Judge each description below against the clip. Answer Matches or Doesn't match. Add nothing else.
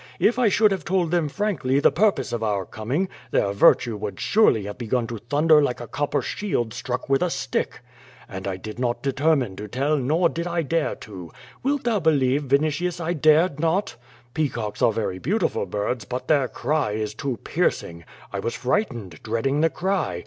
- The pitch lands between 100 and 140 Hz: Matches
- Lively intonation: Matches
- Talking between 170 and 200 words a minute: Matches